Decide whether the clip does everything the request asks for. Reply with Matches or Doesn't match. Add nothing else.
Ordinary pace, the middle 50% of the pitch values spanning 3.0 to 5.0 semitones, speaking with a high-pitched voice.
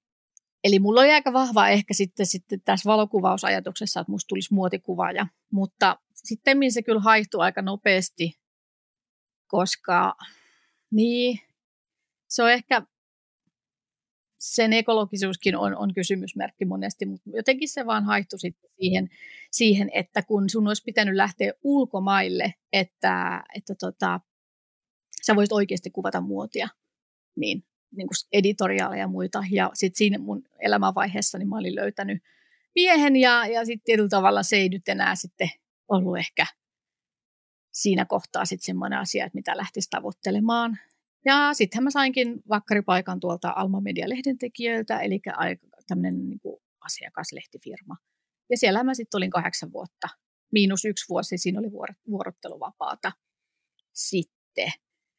Matches